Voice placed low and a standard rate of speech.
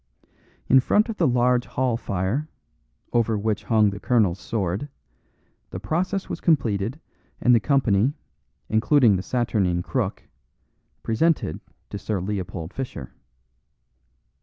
No: low, 115 Hz; slow, 120 wpm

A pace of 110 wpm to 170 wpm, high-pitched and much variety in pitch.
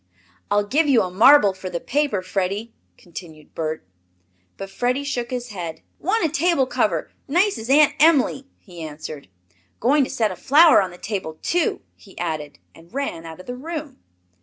No: average, 180 wpm; high, 225 Hz; wide, 8.0 semitones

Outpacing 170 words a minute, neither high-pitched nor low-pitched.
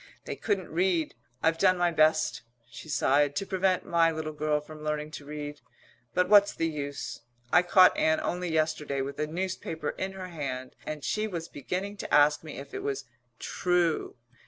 Yes: average, 180 wpm; medium, 160 Hz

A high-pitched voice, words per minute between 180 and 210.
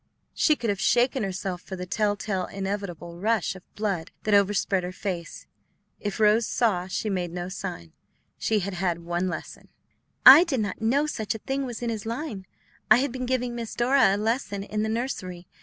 Yes: high, 205 Hz; average, 190 wpm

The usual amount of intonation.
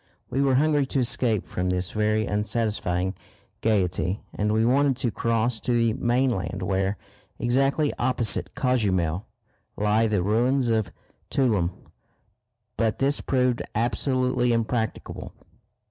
Yes: average, 3.5 semitones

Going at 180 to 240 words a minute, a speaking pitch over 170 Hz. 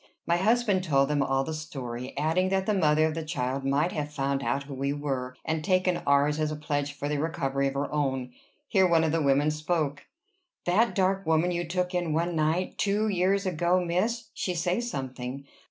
No: fast, 205 wpm; medium, 155 Hz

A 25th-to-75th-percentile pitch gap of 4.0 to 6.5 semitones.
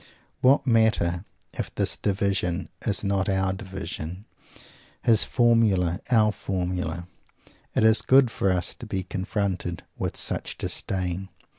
No: average, 3.3 semitones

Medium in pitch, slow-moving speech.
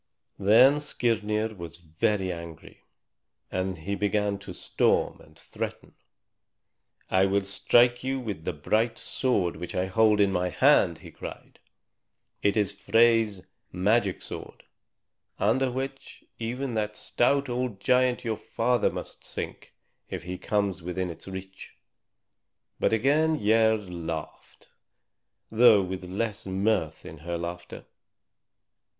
No: low, 105 Hz; slow, 125 wpm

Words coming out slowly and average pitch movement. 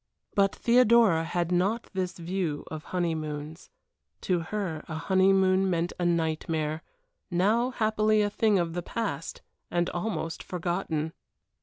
Yes: slow, 130 wpm; average, 3.4 semitones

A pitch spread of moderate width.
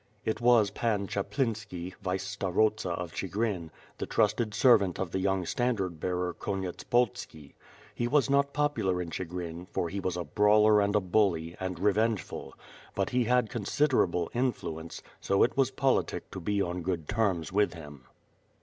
Yes: average, 4.0 semitones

